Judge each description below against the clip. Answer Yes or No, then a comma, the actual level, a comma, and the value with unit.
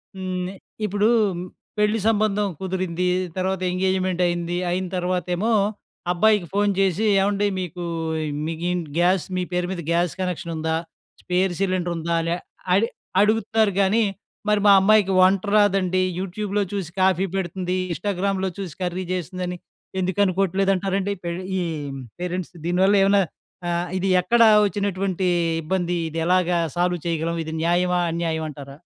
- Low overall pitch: No, medium, 185 Hz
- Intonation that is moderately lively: No, narrow, 2.0 semitones